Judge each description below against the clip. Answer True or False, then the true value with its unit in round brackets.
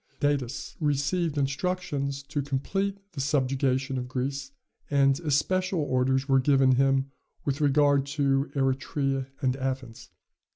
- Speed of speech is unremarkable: False (120 wpm)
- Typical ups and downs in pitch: False (1.5 semitones)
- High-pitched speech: False (140 Hz)